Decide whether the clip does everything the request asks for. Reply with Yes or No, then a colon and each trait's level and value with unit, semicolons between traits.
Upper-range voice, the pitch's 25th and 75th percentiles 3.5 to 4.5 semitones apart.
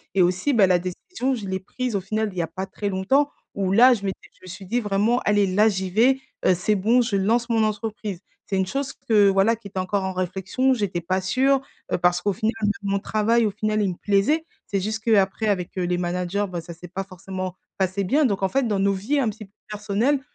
No: high, 200 Hz; average, 3.1 semitones